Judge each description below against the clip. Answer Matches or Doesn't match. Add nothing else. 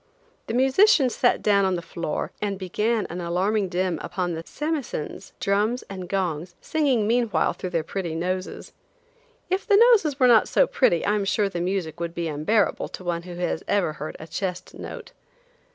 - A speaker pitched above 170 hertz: Matches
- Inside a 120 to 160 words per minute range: Doesn't match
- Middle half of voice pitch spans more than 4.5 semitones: Matches